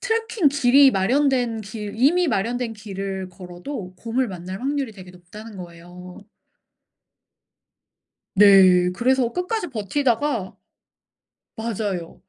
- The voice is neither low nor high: No, high, 220 Hz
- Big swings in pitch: Yes, wide, 6.1 semitones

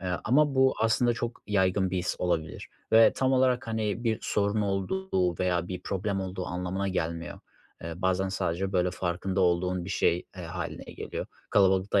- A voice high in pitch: No, very low, 95 Hz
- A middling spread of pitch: Yes, average, 3.3 semitones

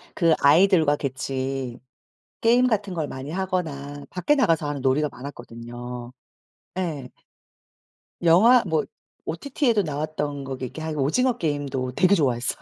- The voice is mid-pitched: Yes, medium, 150 Hz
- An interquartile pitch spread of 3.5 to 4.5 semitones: No, wide, 5.4 semitones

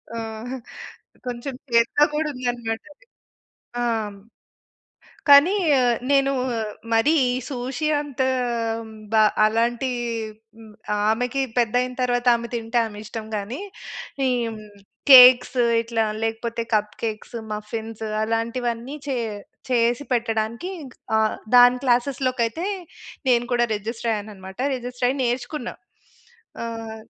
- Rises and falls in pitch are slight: Yes, narrow, 2.0 semitones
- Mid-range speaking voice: No, high, 240 Hz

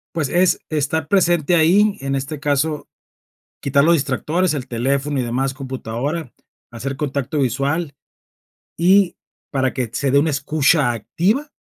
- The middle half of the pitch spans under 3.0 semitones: No, average, 3.5 semitones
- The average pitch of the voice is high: No, medium, 145 Hz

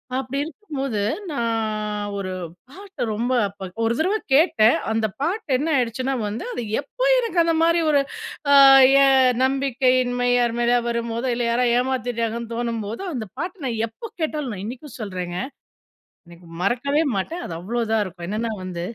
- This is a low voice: No, high, 240 Hz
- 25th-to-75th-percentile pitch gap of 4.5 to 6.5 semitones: No, average, 4.0 semitones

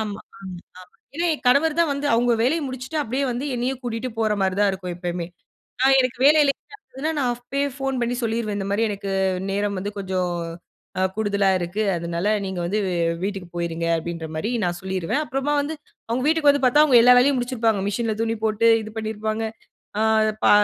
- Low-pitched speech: No, high, 225 Hz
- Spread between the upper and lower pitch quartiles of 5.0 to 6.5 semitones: Yes, wide, 5.5 semitones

